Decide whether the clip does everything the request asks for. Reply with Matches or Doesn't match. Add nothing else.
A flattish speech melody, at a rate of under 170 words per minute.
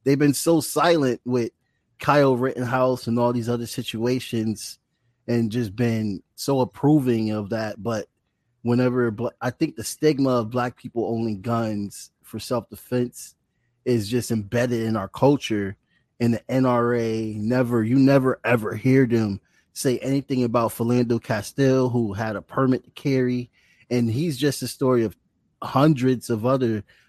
Matches